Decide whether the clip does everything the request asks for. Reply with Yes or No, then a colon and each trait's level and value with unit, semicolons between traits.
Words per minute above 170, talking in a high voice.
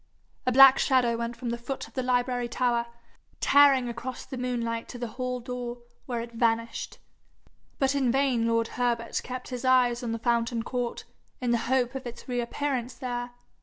Yes: average, 180 wpm; high, 245 Hz